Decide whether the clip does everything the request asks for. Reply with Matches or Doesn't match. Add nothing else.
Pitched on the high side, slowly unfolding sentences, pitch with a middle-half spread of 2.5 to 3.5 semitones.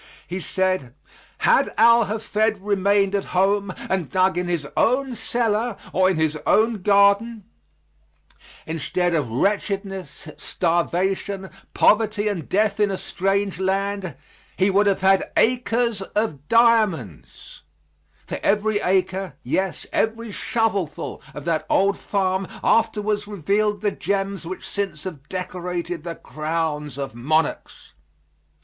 Matches